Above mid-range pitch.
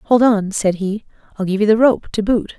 Yes: high, 210 Hz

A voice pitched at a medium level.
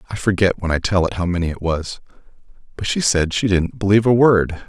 No: very low, 95 Hz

